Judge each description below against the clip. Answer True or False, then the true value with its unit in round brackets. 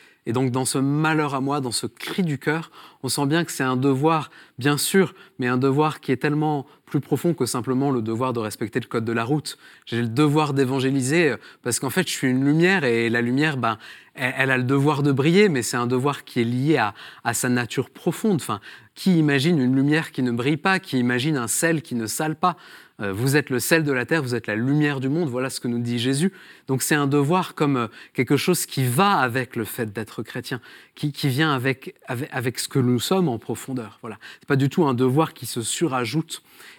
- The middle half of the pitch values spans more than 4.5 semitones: False (3.7 semitones)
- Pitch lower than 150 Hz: True (135 Hz)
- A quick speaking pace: True (240 wpm)